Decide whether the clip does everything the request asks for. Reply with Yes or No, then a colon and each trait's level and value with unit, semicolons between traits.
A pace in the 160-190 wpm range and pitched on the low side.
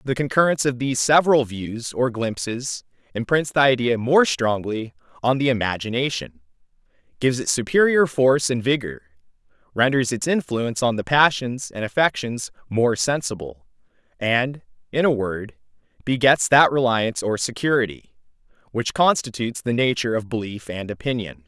No: slow, 135 wpm; low, 120 Hz